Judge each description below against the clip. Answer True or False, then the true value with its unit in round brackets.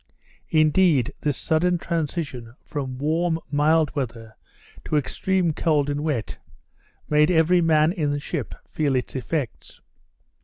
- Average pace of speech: False (125 wpm)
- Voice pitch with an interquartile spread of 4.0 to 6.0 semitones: False (2.7 semitones)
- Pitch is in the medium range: True (150 Hz)